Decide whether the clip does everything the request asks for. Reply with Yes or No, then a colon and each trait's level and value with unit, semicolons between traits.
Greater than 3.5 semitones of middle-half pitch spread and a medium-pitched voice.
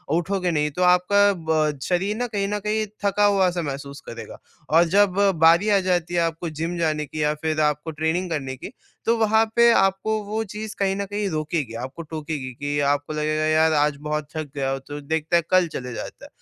Yes: average, 4.6 semitones; medium, 165 Hz